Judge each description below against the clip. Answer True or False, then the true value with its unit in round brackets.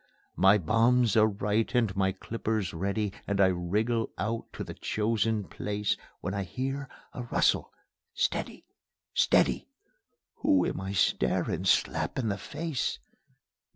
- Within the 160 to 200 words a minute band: False (135 wpm)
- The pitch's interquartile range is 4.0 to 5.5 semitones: False (3.0 semitones)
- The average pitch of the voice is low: True (105 Hz)